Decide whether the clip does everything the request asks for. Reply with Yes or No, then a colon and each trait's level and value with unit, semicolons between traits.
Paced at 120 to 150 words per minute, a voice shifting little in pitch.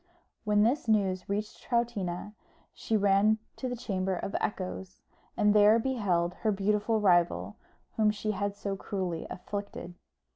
Yes: average, 140 wpm; narrow, 2.2 semitones